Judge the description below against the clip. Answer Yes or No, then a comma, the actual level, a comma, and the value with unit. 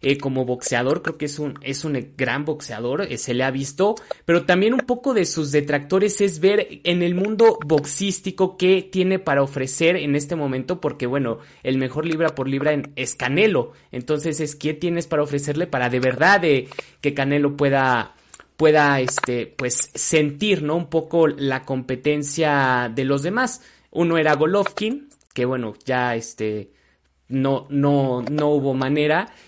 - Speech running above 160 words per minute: Yes, average, 170 wpm